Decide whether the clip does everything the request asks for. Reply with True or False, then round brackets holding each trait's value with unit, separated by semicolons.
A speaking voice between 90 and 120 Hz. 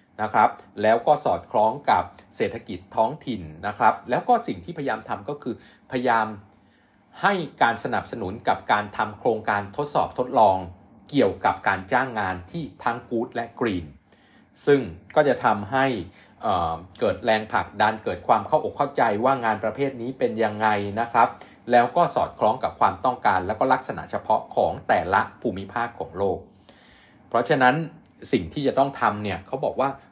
True (115 Hz)